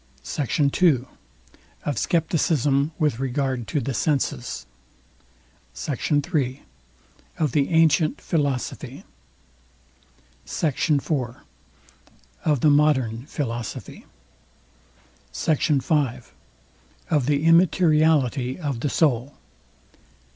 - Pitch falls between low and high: Yes, medium, 145 Hz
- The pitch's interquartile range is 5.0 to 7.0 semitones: No, average, 3.2 semitones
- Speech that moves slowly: Yes, slow, 85 wpm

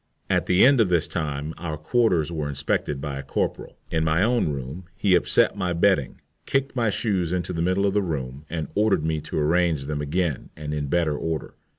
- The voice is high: No, very low, 80 Hz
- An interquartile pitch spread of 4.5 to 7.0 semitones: No, average, 3.8 semitones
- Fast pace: Yes, fast, 210 wpm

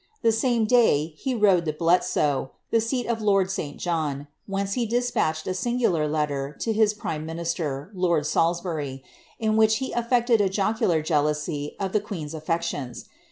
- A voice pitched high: No, medium, 180 Hz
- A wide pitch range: Yes, wide, 6.3 semitones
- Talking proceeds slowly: No, average, 160 wpm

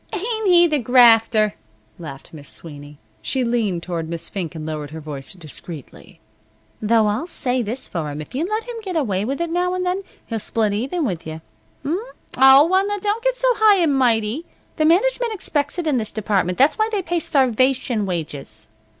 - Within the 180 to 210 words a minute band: Yes, average, 195 wpm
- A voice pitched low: No, high, 245 Hz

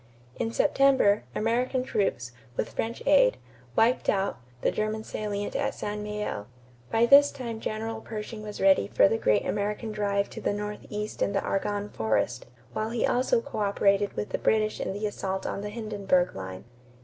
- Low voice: No, high, 210 Hz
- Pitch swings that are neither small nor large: No, narrow, 2.1 semitones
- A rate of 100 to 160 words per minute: No, average, 170 wpm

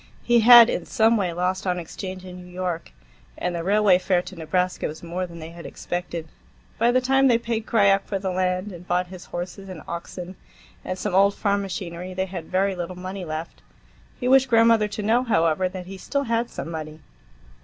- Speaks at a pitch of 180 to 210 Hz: Yes, medium, 185 Hz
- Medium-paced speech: No, fast, 210 wpm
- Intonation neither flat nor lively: Yes, average, 3.0 semitones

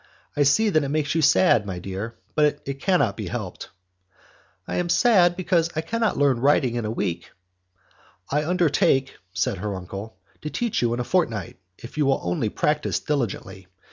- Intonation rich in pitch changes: Yes, wide, 7.0 semitones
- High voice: No, medium, 140 Hz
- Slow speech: No, average, 180 wpm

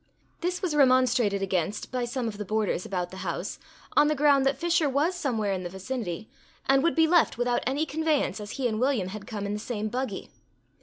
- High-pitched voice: Yes, high, 245 Hz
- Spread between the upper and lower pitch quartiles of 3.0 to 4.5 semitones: No, wide, 5.6 semitones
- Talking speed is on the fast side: Yes, fast, 215 wpm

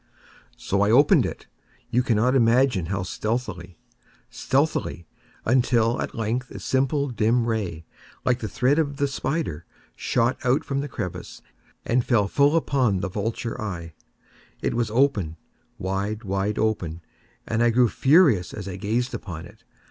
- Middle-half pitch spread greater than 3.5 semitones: Yes, average, 4.7 semitones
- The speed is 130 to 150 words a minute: Yes, average, 140 wpm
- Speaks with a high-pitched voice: No, low, 115 Hz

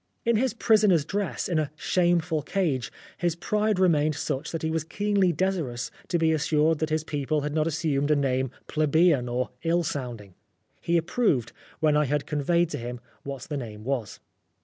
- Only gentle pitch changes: No, average, 3.8 semitones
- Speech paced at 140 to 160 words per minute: No, average, 185 wpm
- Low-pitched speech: No, medium, 155 Hz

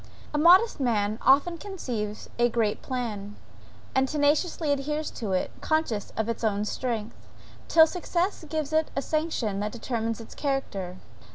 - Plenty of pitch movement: Yes, wide, 6.4 semitones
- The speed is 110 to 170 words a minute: Yes, average, 150 wpm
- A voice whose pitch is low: No, very high, 255 Hz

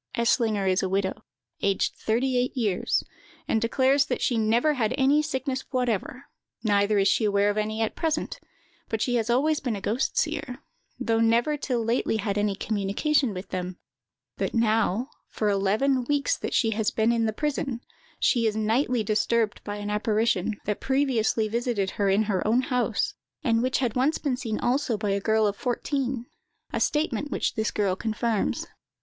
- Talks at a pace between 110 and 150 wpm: No, average, 180 wpm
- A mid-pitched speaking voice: No, high, 225 Hz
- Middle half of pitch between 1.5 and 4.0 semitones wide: Yes, average, 3.6 semitones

